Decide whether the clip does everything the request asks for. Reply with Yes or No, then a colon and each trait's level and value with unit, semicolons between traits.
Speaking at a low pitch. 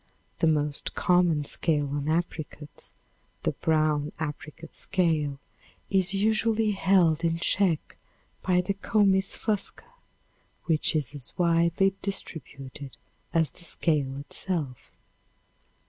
No: medium, 165 Hz